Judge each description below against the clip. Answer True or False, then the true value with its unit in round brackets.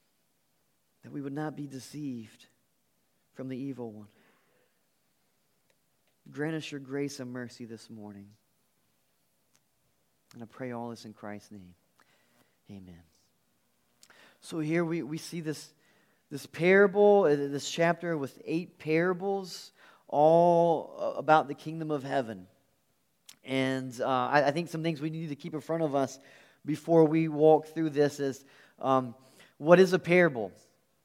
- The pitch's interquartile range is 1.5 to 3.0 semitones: False (4.4 semitones)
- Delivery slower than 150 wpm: True (140 wpm)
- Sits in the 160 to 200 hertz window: False (145 Hz)